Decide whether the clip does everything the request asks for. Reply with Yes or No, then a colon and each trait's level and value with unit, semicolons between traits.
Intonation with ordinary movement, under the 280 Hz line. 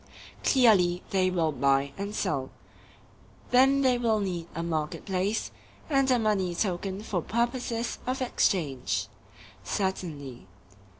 No: wide, 5.9 semitones; high, 190 Hz